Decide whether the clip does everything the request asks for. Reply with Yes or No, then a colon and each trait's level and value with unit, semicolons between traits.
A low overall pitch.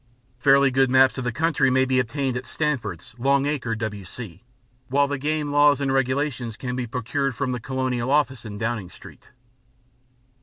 Yes: low, 130 Hz